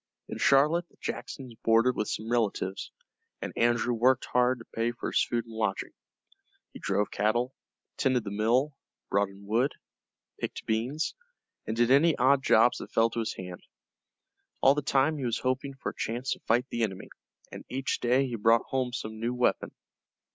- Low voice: Yes, low, 120 Hz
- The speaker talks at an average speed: Yes, average, 185 wpm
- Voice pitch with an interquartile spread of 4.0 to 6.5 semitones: No, average, 2.8 semitones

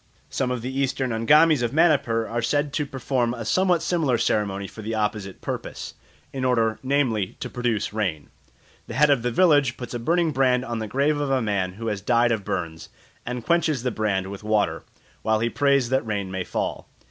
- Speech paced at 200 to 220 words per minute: Yes, fast, 205 wpm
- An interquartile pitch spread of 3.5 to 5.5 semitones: Yes, average, 4.2 semitones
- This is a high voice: No, low, 120 Hz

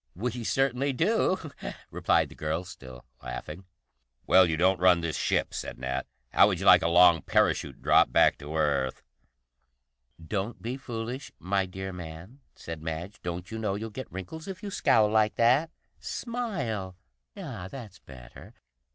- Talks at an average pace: Yes, average, 160 wpm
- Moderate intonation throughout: No, wide, 6.8 semitones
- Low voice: Yes, very low, 95 Hz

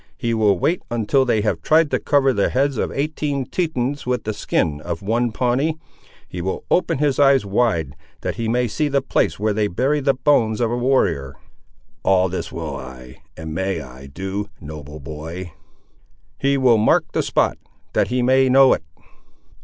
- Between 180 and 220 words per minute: Yes, average, 185 wpm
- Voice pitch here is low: Yes, low, 115 Hz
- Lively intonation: Yes, wide, 7.3 semitones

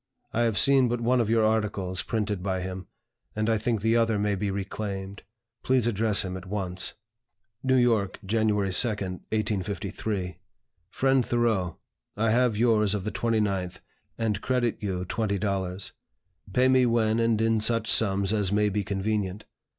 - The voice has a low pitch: Yes, low, 105 Hz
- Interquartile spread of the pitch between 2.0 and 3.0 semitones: Yes, average, 2.7 semitones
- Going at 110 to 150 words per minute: No, average, 160 wpm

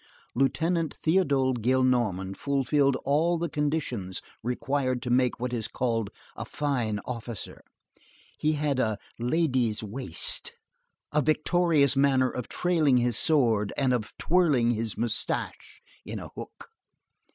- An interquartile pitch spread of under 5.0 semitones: Yes, average, 3.9 semitones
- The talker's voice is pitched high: No, low, 130 Hz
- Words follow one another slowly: Yes, slow, 125 wpm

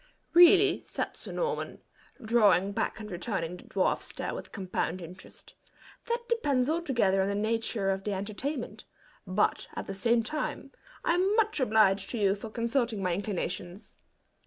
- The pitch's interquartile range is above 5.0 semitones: Yes, wide, 5.6 semitones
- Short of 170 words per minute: Yes, average, 155 wpm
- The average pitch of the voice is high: Yes, high, 215 Hz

